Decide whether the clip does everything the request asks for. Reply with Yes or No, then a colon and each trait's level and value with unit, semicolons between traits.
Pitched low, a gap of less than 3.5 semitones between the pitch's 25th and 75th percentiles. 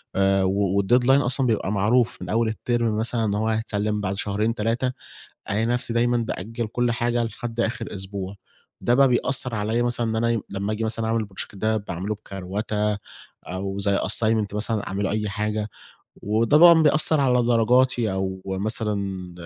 Yes: low, 110 Hz; average, 2.9 semitones